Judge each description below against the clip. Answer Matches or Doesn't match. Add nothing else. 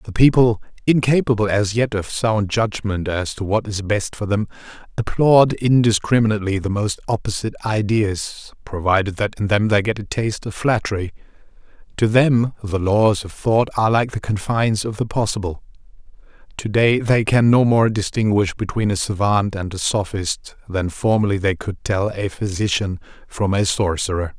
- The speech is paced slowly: Doesn't match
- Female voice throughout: Doesn't match